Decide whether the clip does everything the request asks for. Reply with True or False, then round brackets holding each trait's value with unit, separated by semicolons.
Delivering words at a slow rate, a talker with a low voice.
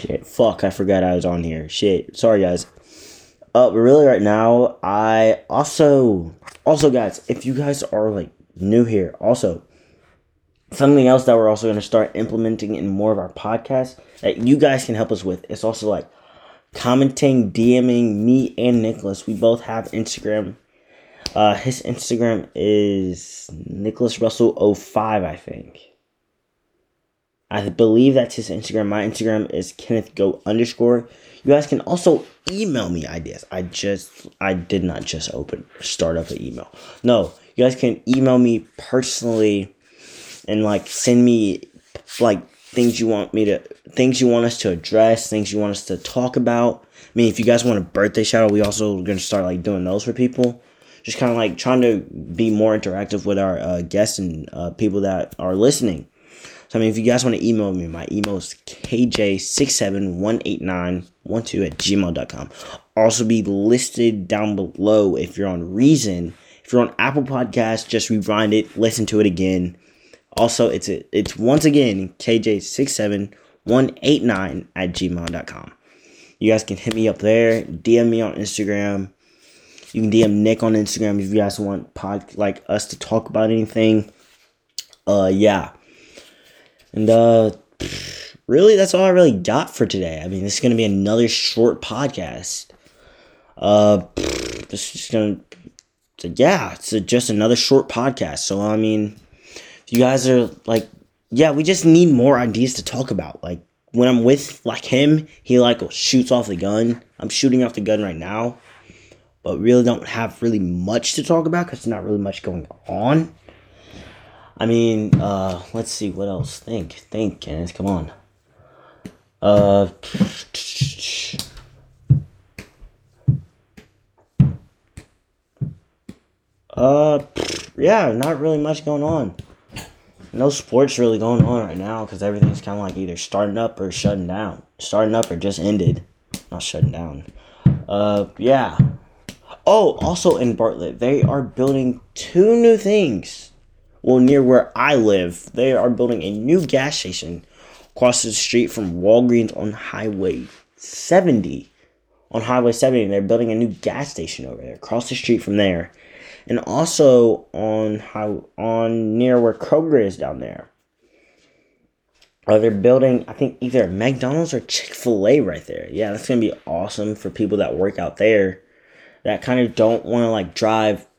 False (165 wpm; 110 Hz)